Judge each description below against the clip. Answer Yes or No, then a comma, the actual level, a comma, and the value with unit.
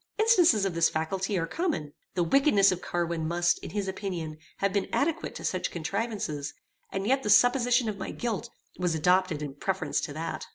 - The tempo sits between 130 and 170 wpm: No, average, 190 wpm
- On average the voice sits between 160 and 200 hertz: Yes, high, 190 Hz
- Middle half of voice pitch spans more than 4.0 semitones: Yes, average, 5.0 semitones